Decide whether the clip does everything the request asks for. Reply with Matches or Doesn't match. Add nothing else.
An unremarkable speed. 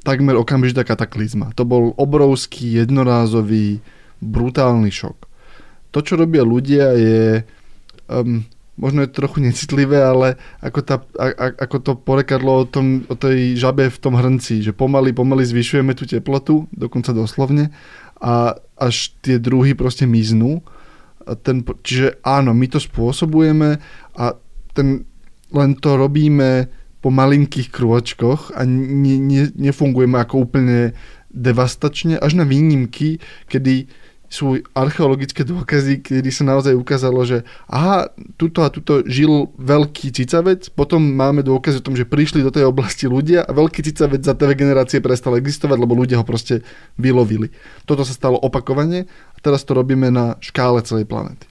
Matches